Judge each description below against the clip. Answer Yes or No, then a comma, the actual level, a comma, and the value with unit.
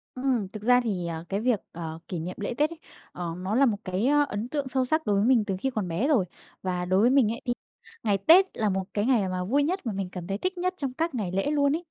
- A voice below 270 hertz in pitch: Yes, high, 220 Hz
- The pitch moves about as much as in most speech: No, wide, 6.4 semitones